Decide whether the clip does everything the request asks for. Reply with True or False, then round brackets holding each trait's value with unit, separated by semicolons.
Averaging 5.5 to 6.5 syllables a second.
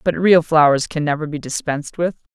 True (5.7 syllables/s)